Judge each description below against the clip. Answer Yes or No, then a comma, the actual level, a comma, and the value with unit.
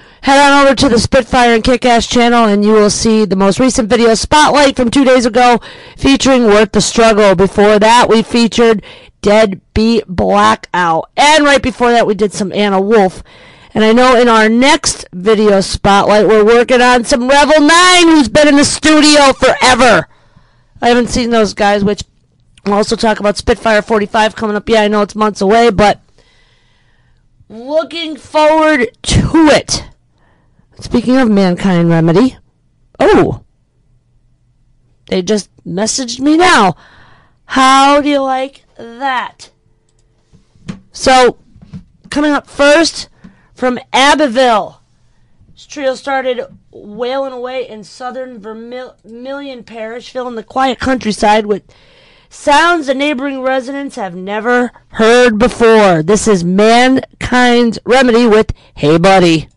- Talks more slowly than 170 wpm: Yes, average, 140 wpm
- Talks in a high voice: Yes, high, 235 Hz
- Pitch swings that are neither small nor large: Yes, average, 4.0 semitones